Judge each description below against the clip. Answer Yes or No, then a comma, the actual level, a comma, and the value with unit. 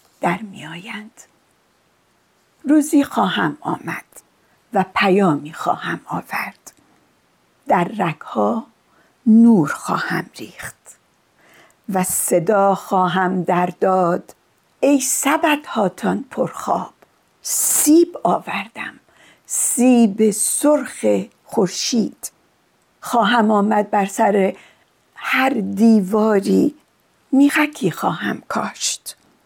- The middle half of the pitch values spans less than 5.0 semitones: No, wide, 5.5 semitones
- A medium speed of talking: No, slow, 75 wpm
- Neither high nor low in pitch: No, high, 215 Hz